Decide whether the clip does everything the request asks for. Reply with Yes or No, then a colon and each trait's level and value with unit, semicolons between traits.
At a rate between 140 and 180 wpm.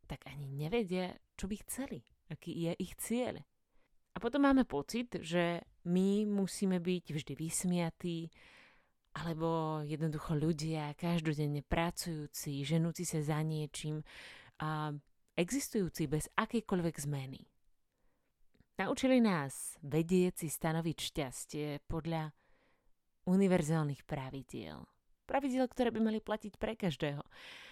No: slow, 110 wpm